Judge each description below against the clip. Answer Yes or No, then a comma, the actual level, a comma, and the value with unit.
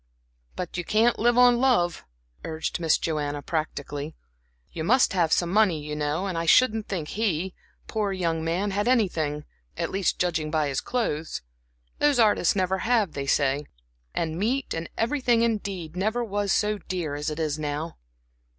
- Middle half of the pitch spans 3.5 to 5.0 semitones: No, wide, 5.6 semitones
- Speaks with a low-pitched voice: No, medium, 180 Hz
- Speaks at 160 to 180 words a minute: Yes, average, 170 wpm